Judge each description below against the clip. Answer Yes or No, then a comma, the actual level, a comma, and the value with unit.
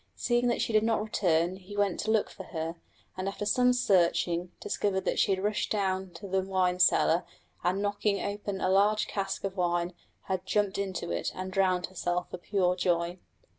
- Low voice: No, high, 190 Hz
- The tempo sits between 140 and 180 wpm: No, average, 195 wpm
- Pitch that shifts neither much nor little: No, narrow, 2.2 semitones